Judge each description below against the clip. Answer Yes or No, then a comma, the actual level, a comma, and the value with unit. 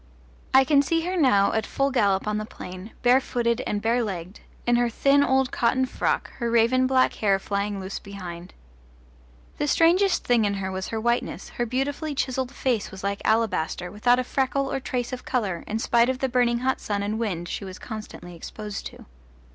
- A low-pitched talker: No, high, 235 Hz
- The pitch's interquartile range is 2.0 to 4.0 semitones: No, average, 4.5 semitones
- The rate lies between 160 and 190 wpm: No, average, 200 wpm